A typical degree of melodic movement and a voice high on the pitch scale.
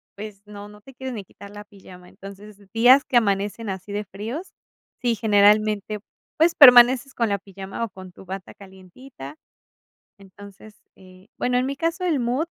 Yes: average, 3.8 semitones; high, 210 Hz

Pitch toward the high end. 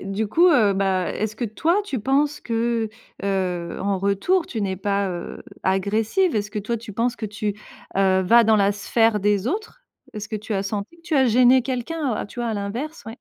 Yes: high, 215 Hz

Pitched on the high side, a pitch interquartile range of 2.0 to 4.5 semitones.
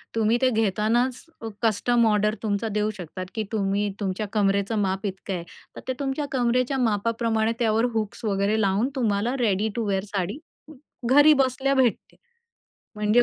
Yes: high, 220 Hz; average, 3.1 semitones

